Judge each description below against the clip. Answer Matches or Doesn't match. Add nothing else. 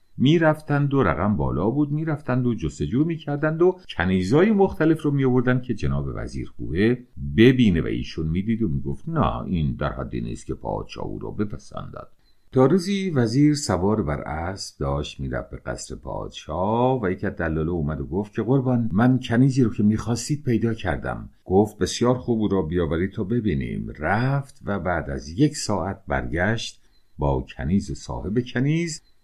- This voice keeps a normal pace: Doesn't match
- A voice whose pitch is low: Matches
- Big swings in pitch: Matches